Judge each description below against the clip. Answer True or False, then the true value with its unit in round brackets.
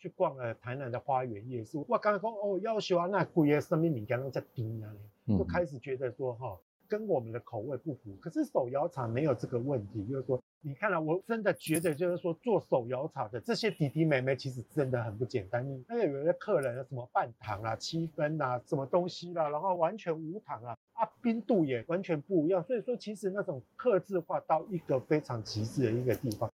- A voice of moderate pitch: True (150 Hz)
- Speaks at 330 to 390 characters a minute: True (340 characters per minute)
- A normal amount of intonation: False (6.4 semitones)